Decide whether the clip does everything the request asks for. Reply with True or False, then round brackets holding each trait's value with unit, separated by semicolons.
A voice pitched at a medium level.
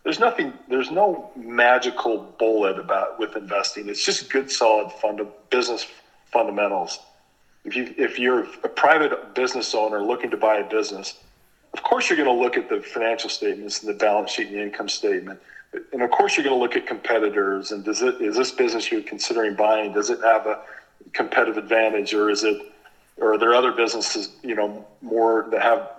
False (115 Hz)